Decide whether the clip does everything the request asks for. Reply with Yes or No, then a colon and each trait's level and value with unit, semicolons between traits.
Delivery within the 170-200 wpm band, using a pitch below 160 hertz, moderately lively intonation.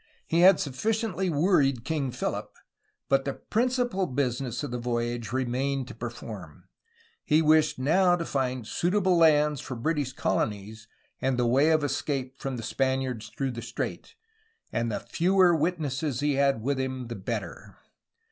No: average, 155 wpm; low, 135 Hz; average, 4.7 semitones